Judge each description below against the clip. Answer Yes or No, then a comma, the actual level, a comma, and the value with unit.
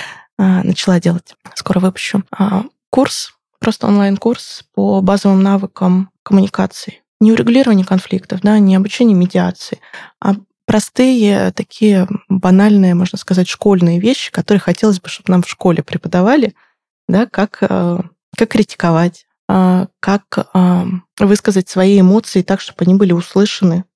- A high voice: Yes, high, 195 Hz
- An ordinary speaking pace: Yes, average, 120 wpm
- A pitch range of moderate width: No, narrow, 2.2 semitones